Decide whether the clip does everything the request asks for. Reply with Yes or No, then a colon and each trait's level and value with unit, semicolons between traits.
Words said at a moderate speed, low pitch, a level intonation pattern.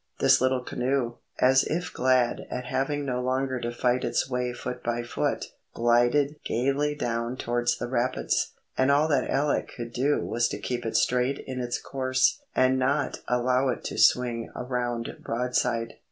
Yes: average, 170 wpm; low, 125 Hz; narrow, 1.6 semitones